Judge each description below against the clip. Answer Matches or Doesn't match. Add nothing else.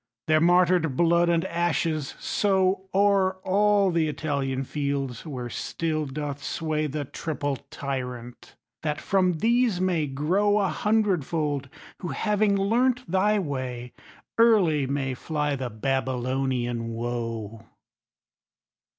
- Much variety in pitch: Matches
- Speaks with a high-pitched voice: Doesn't match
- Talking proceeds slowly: Matches